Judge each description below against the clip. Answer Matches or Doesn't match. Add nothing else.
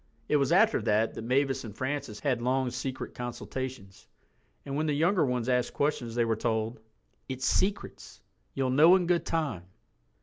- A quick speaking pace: Doesn't match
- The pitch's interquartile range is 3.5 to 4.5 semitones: Matches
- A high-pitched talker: Doesn't match